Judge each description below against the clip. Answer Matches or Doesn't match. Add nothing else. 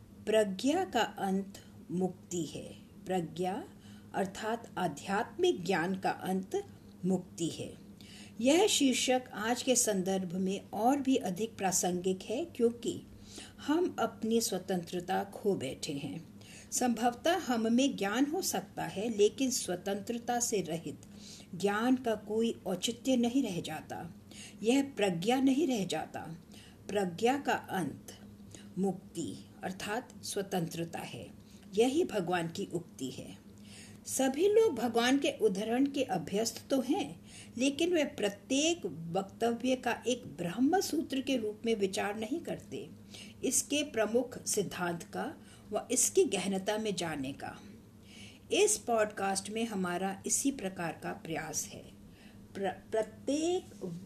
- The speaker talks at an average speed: Doesn't match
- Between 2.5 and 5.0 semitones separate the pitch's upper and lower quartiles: Doesn't match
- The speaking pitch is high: Matches